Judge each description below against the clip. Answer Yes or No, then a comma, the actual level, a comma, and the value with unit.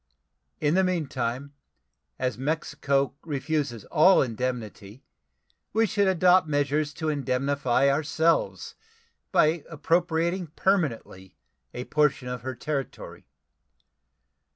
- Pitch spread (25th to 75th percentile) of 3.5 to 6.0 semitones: Yes, average, 4.2 semitones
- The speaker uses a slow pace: Yes, slow, 95 wpm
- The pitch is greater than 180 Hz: No, medium, 145 Hz